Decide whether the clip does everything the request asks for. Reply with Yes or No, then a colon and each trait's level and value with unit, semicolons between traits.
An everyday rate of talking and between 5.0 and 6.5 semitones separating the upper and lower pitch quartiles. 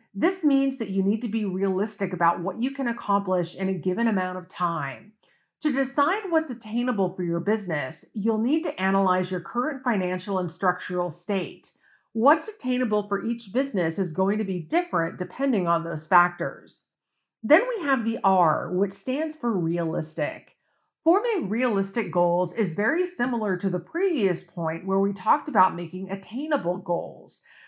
Yes: average, 165 wpm; wide, 5.5 semitones